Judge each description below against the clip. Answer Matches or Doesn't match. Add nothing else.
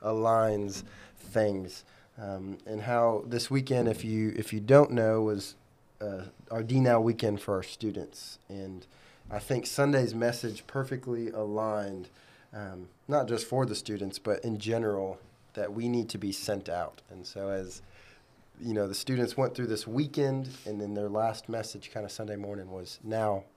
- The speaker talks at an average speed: Matches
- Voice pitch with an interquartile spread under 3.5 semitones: Matches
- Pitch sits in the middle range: Doesn't match